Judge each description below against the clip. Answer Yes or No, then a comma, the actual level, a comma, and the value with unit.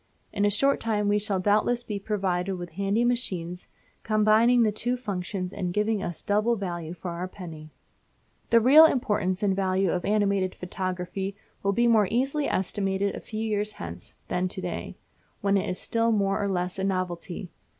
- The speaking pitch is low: No, high, 200 Hz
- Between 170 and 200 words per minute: Yes, average, 180 wpm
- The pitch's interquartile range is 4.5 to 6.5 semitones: No, average, 2.8 semitones